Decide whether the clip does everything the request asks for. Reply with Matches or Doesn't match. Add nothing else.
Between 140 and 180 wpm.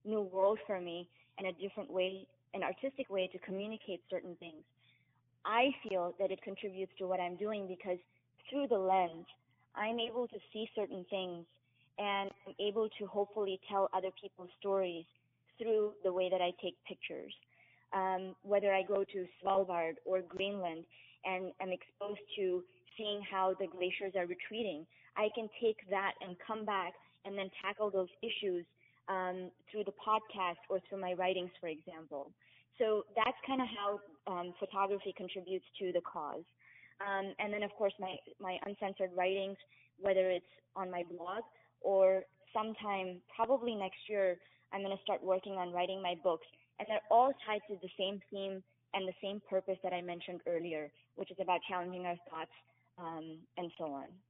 Matches